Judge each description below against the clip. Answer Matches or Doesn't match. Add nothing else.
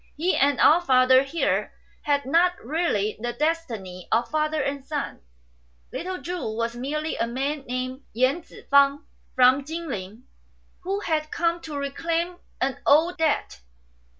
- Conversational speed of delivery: Matches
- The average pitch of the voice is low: Doesn't match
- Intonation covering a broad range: Doesn't match